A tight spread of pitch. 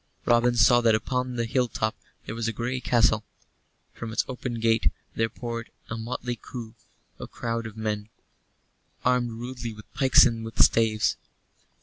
Yes: narrow, 1.6 semitones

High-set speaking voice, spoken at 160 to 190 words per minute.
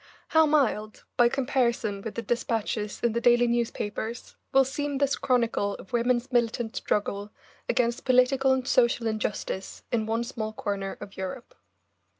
No: high, 235 Hz; average, 150 wpm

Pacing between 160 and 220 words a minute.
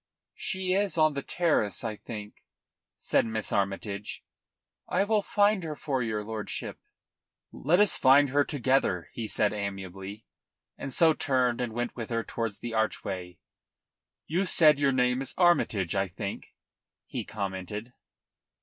No: average, 145 wpm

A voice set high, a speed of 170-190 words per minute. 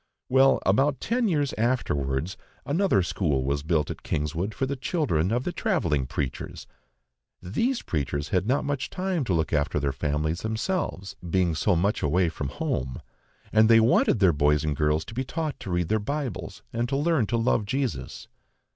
No: low, 100 Hz; average, 180 wpm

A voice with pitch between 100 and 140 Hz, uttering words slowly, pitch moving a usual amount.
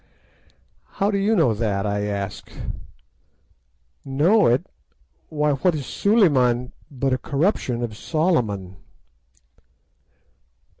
No: low, 135 Hz; slow, 100 wpm; wide, 7.2 semitones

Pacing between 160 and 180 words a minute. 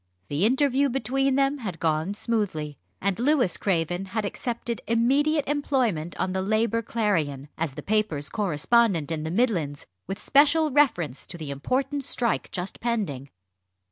No: average, 145 wpm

